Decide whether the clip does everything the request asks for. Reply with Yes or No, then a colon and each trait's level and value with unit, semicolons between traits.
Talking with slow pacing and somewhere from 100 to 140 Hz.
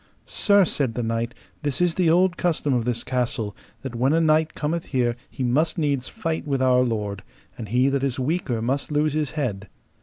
No: fast, 205 wpm; low, 135 Hz